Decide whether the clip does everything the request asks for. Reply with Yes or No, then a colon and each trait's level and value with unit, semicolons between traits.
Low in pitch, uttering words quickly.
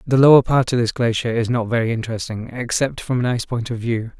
Yes: low, 120 Hz; fast, 245 wpm